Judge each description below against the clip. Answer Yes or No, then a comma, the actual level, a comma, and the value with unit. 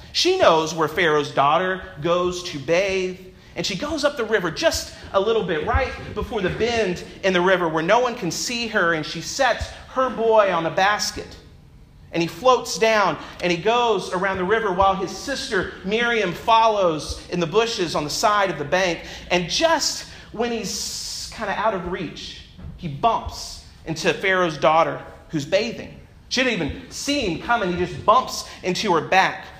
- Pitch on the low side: No, high, 190 Hz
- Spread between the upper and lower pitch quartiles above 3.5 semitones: Yes, average, 4.9 semitones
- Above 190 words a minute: No, average, 185 wpm